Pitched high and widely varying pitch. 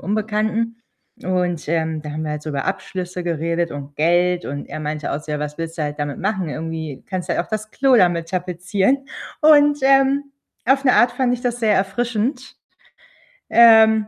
No: medium, 180 Hz; wide, 6.2 semitones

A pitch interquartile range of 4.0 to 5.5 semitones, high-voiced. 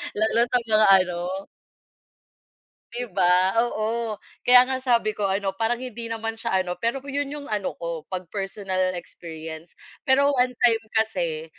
Yes: average, 4.5 semitones; high, 215 Hz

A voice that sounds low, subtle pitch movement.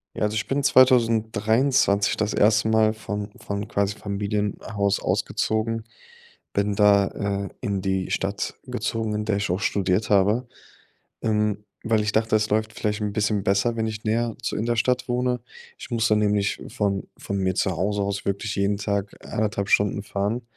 Yes: low, 105 Hz; narrow, 1.8 semitones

